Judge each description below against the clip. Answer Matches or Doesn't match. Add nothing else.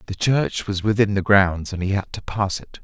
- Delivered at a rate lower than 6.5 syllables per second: Matches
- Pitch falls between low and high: Doesn't match